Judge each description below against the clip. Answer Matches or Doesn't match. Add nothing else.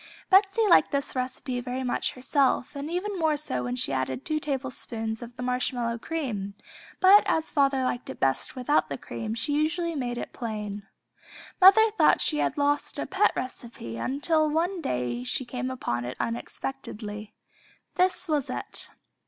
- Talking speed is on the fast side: Doesn't match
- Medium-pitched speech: Doesn't match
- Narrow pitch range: Doesn't match